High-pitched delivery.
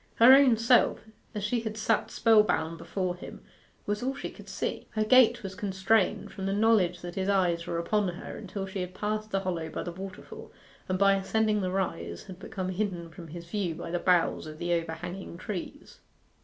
Yes: high, 195 Hz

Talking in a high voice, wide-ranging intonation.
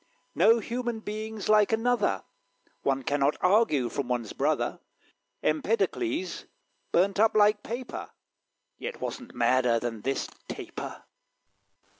Yes: high, 205 Hz; wide, 8.8 semitones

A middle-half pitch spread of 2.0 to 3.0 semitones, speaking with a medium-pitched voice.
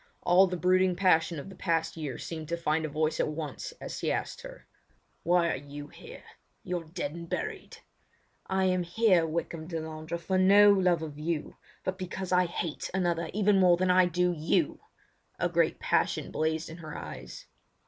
Yes: narrow, 2.6 semitones; medium, 170 Hz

